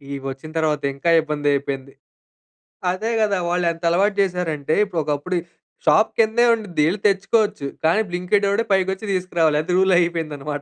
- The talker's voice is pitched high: No, medium, 175 Hz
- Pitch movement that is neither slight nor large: Yes, average, 4.5 semitones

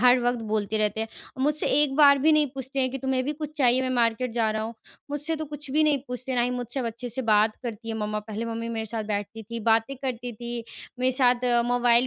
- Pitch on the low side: No, high, 245 Hz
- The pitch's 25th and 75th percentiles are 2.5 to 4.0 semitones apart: Yes, average, 2.9 semitones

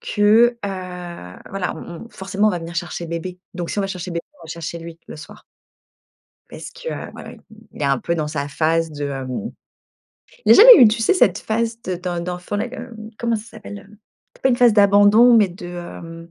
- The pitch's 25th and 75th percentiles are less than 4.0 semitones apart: No, average, 4.5 semitones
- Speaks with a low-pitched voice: No, medium, 185 Hz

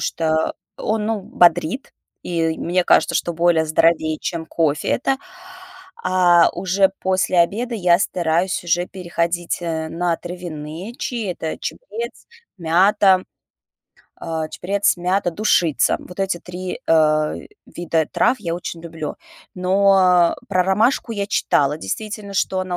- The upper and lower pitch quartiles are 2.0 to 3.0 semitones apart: Yes, average, 2.7 semitones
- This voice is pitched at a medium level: Yes, medium, 175 Hz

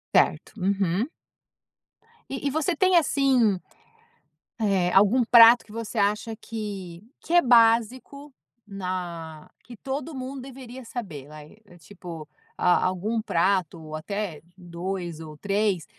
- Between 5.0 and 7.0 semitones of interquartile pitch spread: Yes, wide, 5.5 semitones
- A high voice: Yes, high, 205 Hz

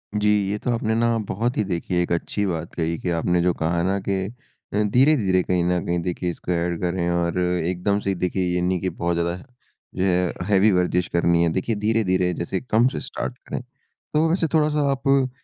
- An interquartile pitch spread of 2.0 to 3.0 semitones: No, average, 3.7 semitones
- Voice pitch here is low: Yes, very low, 90 Hz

